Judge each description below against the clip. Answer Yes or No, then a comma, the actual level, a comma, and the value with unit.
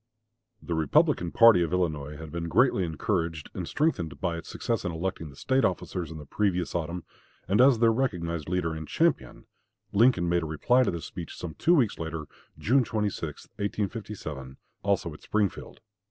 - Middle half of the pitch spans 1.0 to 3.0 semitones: No, average, 4.8 semitones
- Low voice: Yes, very low, 85 Hz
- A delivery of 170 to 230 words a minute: Yes, average, 175 wpm